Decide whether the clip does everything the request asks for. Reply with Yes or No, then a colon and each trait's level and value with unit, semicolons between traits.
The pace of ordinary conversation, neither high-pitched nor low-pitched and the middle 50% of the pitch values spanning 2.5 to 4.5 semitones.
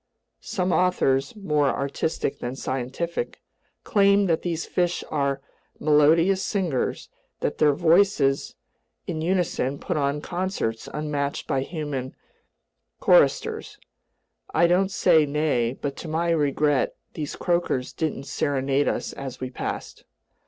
No: slow, 115 wpm; medium, 150 Hz; average, 4.2 semitones